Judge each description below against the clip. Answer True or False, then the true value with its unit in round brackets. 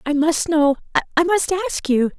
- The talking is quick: False (190 wpm)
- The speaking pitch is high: True (315 Hz)